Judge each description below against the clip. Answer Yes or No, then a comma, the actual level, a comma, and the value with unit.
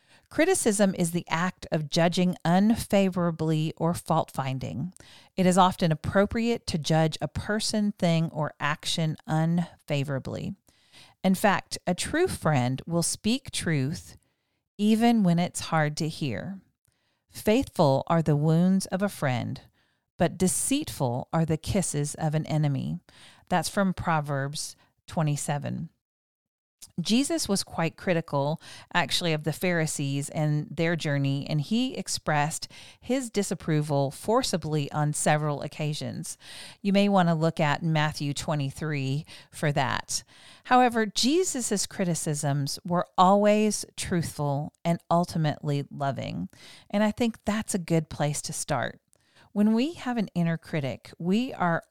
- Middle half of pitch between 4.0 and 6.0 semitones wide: Yes, average, 4.6 semitones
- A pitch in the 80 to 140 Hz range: No, medium, 165 Hz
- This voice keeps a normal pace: No, slow, 130 wpm